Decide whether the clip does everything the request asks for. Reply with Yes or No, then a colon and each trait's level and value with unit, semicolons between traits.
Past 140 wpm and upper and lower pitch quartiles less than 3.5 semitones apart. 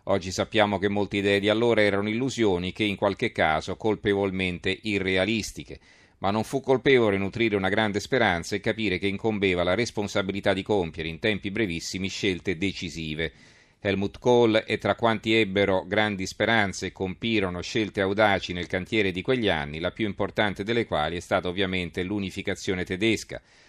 Yes: average, 160 wpm; narrow, 2.5 semitones